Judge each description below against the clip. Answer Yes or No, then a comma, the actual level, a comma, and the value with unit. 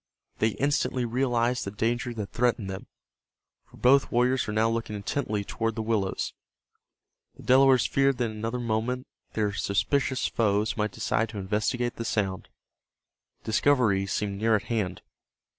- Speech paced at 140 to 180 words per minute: Yes, average, 150 wpm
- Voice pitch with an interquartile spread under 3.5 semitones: Yes, average, 2.9 semitones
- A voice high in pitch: No, low, 115 Hz